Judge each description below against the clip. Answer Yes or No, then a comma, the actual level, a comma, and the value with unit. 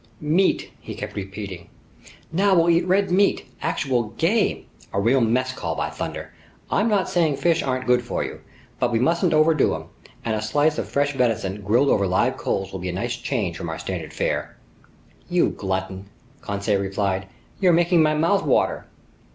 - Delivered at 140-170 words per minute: No, average, 180 wpm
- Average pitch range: No, wide, 8.9 semitones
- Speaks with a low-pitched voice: Yes, low, 125 Hz